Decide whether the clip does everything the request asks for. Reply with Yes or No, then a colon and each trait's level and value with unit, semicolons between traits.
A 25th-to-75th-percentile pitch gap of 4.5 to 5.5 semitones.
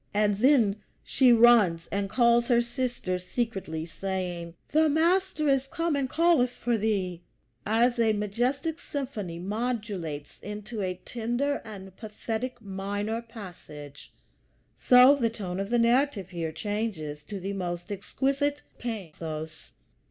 Yes: average, 4.9 semitones